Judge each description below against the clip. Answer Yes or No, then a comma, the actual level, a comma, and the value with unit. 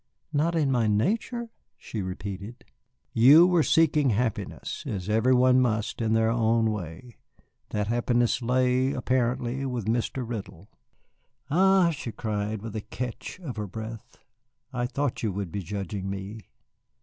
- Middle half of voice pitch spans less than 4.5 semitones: Yes, average, 3.5 semitones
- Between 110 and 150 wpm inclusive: Yes, average, 145 wpm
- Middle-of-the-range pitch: No, low, 115 Hz